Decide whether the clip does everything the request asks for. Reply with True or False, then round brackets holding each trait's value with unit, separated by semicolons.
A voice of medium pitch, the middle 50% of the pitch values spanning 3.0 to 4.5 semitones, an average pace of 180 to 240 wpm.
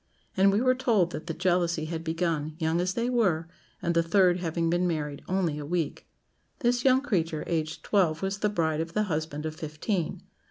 True (170 Hz; 3.4 semitones; 200 wpm)